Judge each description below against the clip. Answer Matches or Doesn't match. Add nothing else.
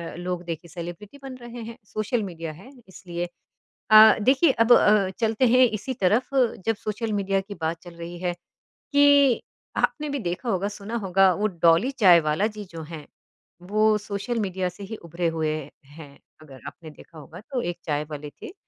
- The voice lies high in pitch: Matches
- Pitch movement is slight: Doesn't match